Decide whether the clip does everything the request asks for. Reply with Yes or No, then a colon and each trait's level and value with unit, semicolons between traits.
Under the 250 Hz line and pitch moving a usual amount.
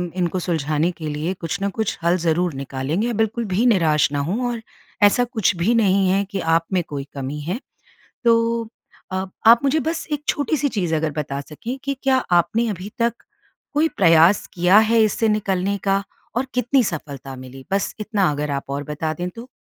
No: medium, 185 Hz; wide, 6.6 semitones